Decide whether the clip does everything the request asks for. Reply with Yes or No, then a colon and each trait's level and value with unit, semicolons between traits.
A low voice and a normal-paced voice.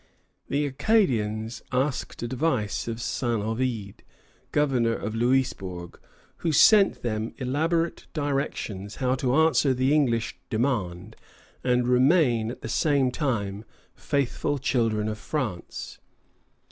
No: low, 125 Hz; slow, 110 wpm